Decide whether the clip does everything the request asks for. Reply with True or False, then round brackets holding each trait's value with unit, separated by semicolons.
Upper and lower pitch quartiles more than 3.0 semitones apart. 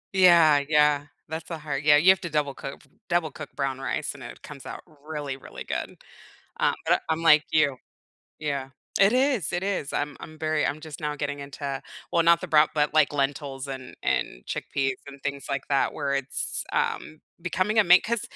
False (2.6 semitones)